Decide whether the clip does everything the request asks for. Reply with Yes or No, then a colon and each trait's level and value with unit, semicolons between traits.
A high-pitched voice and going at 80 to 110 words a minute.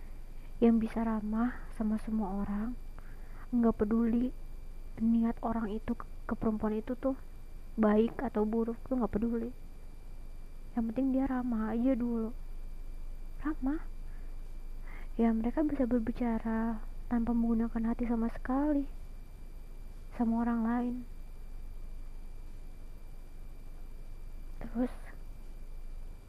Yes: high, 230 Hz; average, 95 wpm